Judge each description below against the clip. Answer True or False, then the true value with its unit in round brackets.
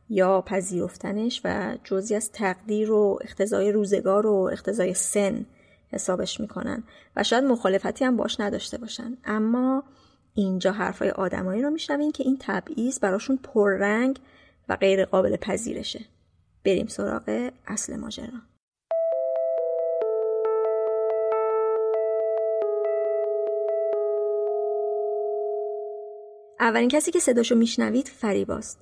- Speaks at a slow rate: True (95 wpm)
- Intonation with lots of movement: False (3.0 semitones)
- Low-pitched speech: False (215 Hz)